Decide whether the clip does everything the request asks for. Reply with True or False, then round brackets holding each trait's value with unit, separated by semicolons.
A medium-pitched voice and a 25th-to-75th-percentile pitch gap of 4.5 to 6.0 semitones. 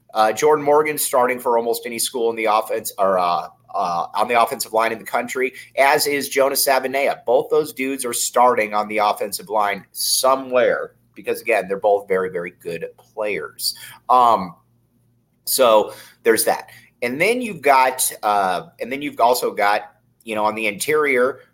False (130 Hz; 4.8 semitones)